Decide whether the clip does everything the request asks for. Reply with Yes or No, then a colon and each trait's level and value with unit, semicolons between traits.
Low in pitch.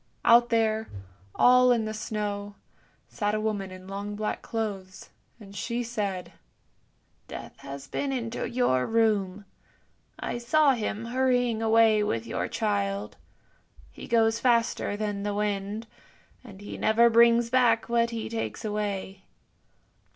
No: high, 220 Hz